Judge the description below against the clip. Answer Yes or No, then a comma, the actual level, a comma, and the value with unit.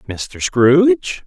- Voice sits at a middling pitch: Yes, medium, 155 Hz